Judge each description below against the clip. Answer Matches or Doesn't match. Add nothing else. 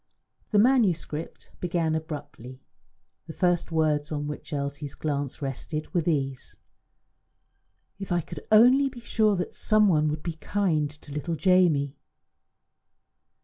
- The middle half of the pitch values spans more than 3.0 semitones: Matches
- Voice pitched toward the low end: Doesn't match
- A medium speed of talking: Doesn't match